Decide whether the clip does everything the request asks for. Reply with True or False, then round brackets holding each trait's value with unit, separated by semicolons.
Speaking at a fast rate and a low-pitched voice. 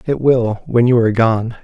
True (220 wpm; 120 Hz)